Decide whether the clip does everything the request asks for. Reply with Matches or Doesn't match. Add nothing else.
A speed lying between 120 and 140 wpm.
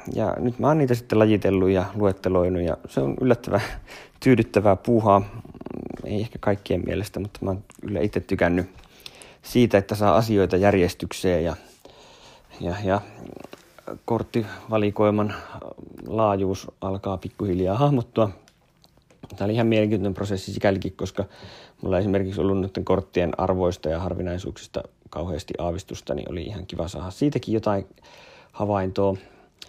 Matches